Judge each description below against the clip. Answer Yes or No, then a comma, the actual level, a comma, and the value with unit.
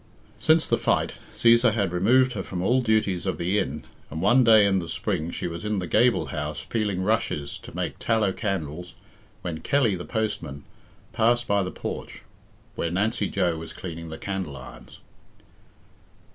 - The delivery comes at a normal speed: Yes, average, 175 wpm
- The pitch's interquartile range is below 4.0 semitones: No, average, 4.7 semitones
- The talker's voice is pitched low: Yes, very low, 95 Hz